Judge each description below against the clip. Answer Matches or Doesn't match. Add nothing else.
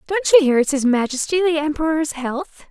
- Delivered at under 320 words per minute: Matches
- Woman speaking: Matches